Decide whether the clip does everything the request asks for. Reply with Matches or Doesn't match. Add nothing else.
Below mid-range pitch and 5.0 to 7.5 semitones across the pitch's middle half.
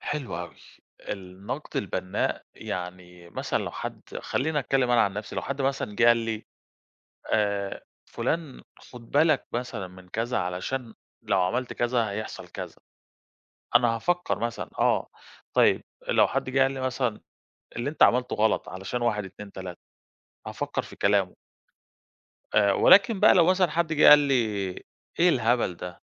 Matches